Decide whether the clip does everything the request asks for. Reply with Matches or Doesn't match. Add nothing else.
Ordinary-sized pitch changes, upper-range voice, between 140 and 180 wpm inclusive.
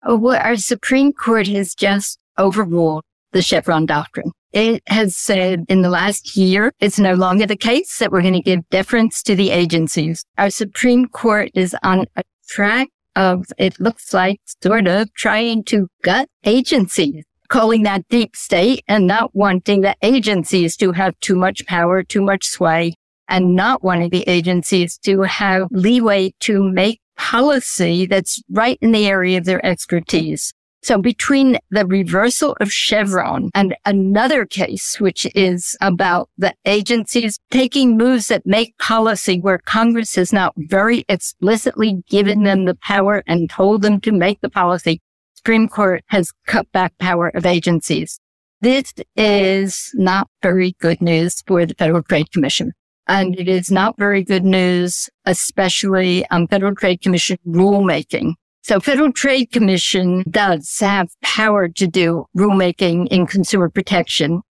Matches